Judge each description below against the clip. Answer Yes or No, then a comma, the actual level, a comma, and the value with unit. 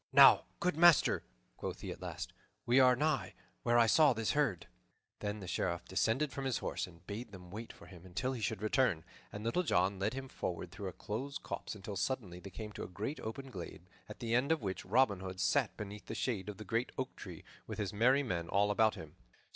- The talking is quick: Yes, fast, 225 wpm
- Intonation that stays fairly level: No, average, 5.3 semitones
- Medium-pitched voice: No, low, 105 Hz